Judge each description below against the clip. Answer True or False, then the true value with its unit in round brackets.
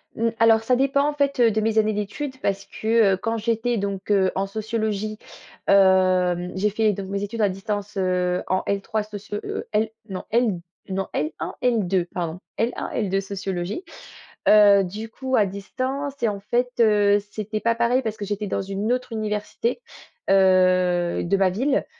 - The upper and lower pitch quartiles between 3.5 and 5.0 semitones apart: False (2.8 semitones)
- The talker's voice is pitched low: False (210 Hz)